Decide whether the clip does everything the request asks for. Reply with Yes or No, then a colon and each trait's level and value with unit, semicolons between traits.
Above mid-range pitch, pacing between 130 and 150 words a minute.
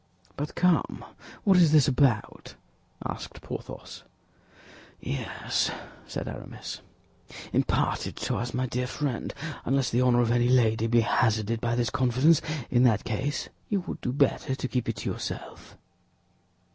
No: low, 125 Hz; average, 145 wpm